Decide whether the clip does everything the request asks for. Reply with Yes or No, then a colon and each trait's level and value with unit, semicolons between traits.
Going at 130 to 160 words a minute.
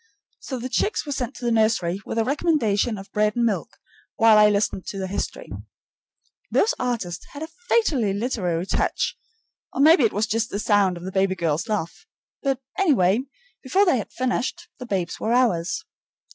No: average, 185 wpm